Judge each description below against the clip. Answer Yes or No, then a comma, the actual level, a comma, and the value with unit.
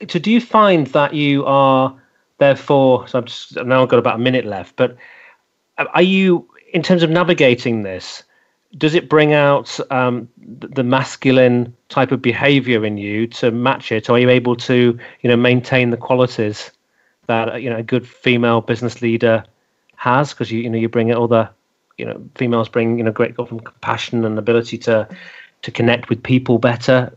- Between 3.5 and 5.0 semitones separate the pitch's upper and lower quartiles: No, narrow, 2.4 semitones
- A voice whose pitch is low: Yes, low, 125 Hz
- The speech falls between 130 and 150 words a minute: No, average, 185 wpm